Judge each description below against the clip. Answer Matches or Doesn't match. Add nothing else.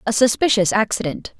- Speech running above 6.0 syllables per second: Doesn't match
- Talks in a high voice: Matches